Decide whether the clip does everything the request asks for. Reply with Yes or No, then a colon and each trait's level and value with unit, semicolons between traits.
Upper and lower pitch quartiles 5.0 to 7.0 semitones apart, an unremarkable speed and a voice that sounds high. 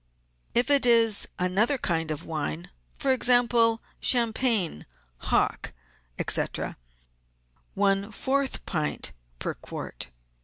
No: wide, 5.4 semitones; slow, 100 wpm; high, 225 Hz